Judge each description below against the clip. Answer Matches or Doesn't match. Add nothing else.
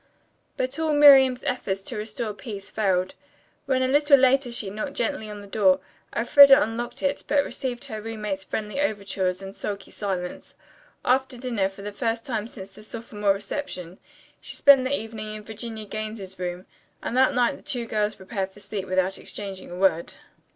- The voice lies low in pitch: Doesn't match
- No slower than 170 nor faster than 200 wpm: Matches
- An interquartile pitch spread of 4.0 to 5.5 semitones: Matches